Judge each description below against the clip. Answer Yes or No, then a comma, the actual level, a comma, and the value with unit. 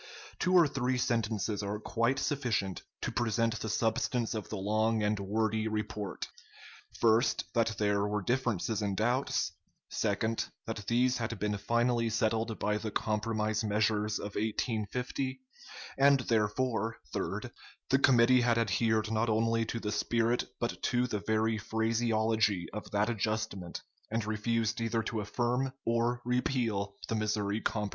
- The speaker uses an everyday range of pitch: No, narrow, 1.9 semitones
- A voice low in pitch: Yes, low, 110 Hz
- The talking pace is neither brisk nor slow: Yes, average, 145 wpm